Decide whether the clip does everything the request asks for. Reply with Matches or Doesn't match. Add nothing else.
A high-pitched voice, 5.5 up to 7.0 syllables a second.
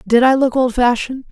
Matches